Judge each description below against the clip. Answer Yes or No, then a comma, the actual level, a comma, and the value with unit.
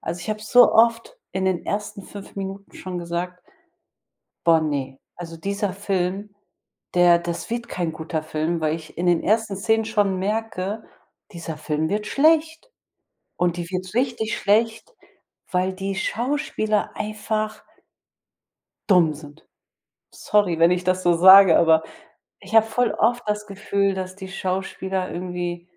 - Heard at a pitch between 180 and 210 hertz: Yes, high, 190 Hz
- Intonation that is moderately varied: Yes, average, 3.6 semitones